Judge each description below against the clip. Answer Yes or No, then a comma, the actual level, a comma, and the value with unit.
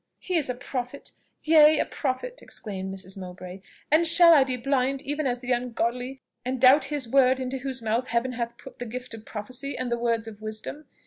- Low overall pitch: No, very high, 255 Hz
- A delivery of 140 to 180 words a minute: No, fast, 205 wpm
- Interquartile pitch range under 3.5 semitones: Yes, average, 2.8 semitones